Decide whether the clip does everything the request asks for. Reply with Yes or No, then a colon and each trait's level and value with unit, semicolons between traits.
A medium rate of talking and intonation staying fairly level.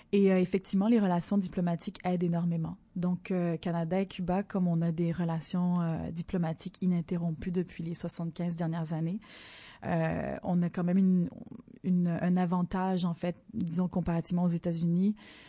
Yes: average, 160 wpm; narrow, 1.6 semitones